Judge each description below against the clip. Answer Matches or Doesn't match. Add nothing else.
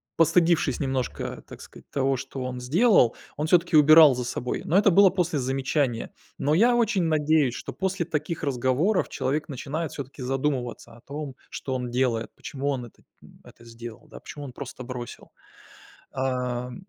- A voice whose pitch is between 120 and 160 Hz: Matches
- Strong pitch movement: Doesn't match